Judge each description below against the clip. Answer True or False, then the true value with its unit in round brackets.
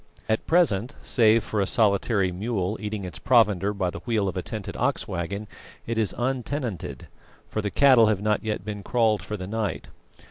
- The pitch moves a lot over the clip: False (2.7 semitones)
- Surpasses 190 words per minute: False (185 wpm)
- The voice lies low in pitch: True (105 Hz)